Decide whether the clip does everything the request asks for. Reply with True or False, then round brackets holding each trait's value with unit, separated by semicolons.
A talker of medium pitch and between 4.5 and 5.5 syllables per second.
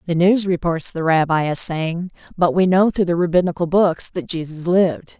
True (170 Hz; 5.1 syllables/s)